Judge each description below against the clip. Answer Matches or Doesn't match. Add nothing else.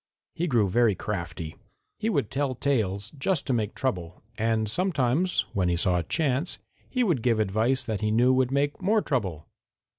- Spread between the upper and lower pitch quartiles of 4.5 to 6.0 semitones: Matches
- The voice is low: Matches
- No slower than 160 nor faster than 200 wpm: Matches